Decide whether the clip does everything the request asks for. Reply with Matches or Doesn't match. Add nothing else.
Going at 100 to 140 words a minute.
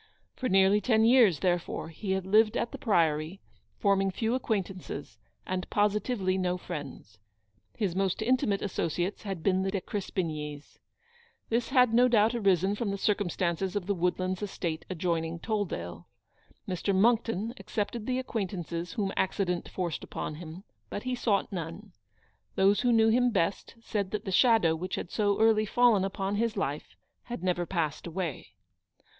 Doesn't match